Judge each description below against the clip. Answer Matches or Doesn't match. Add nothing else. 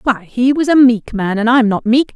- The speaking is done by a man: Doesn't match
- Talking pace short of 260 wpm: Doesn't match